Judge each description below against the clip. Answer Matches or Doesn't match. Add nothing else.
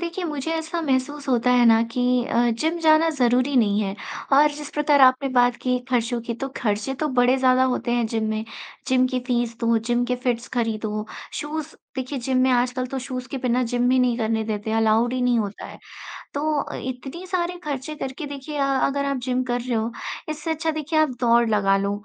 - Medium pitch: Doesn't match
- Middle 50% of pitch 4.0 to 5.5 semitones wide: Doesn't match